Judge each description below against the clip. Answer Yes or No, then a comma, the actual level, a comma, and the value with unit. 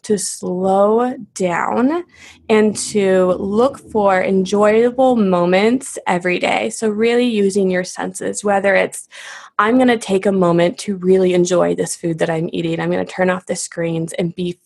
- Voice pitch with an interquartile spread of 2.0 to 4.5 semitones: Yes, average, 3.3 semitones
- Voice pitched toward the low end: No, high, 190 Hz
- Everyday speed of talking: Yes, average, 170 wpm